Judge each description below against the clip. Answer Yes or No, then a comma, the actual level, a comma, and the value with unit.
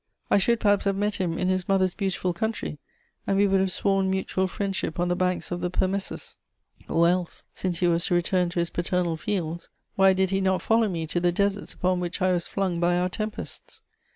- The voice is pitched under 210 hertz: Yes, medium, 185 Hz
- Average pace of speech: No, fast, 220 wpm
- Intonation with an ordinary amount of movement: No, narrow, 1.8 semitones